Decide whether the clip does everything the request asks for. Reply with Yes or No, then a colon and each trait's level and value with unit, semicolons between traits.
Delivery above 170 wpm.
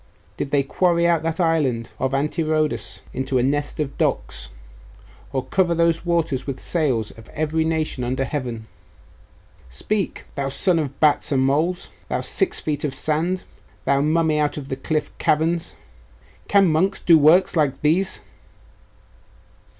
No: average, 150 wpm